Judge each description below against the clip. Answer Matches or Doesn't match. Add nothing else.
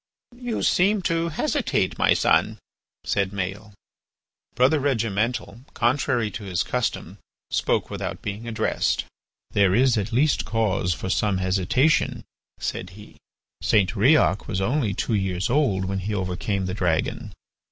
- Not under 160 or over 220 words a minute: Doesn't match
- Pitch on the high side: Doesn't match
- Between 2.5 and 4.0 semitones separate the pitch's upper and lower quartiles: Doesn't match